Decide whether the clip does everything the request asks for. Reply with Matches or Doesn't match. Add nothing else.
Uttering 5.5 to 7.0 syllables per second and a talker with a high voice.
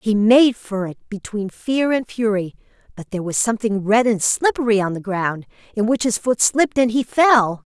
Doesn't match